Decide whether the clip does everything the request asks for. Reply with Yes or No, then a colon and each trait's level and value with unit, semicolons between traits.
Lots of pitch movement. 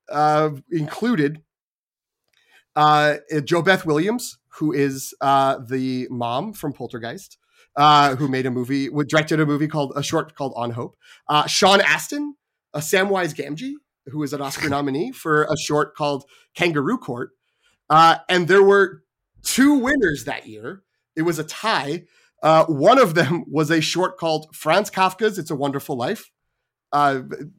No: average, 4.5 semitones